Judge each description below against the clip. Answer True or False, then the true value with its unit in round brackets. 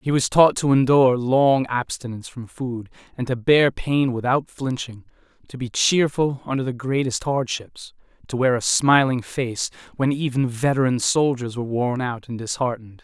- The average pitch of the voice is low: True (130 Hz)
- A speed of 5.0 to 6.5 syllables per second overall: False (4.8 syllables/s)